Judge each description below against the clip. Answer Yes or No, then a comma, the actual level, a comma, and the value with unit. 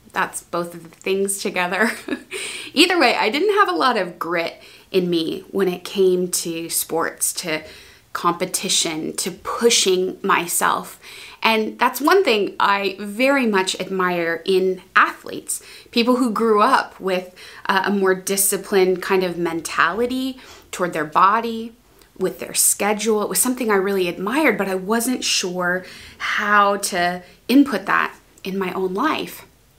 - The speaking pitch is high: Yes, high, 195 Hz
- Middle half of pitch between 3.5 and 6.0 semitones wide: Yes, average, 3.9 semitones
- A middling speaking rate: Yes, average, 145 wpm